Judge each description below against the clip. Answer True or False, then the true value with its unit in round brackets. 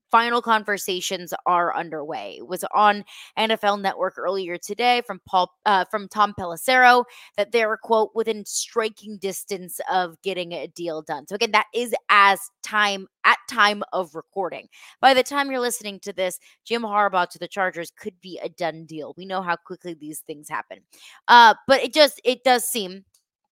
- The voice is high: True (200 Hz)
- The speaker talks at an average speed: True (180 wpm)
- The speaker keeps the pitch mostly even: False (3.7 semitones)